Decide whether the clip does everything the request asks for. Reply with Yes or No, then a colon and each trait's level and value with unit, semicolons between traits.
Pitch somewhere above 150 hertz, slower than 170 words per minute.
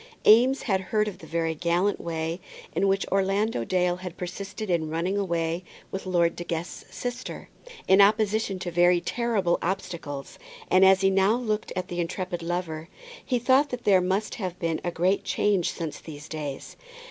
No: medium, 185 Hz; average, 175 wpm